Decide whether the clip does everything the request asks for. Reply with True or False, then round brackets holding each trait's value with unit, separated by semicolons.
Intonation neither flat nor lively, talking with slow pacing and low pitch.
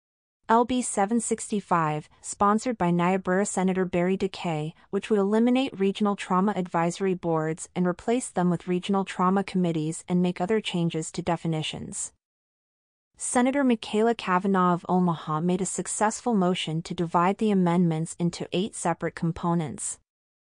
False (3.0 semitones; 130 wpm; 180 Hz)